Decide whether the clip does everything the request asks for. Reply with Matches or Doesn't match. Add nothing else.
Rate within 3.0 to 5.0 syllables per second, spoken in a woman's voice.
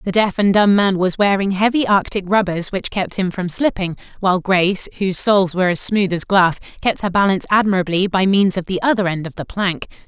Doesn't match